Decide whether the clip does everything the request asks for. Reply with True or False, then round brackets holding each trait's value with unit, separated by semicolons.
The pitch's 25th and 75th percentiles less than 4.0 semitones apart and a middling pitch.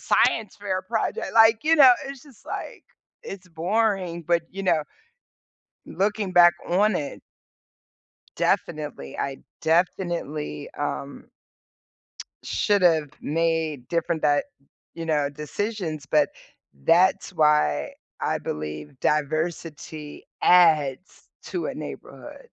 False (4.5 semitones; 165 Hz)